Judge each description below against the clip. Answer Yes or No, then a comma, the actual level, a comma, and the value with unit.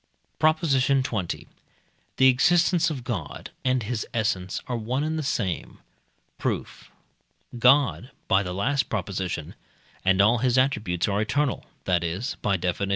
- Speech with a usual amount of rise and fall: No, wide, 5.7 semitones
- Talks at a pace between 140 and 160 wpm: Yes, average, 145 wpm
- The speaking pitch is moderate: No, low, 120 Hz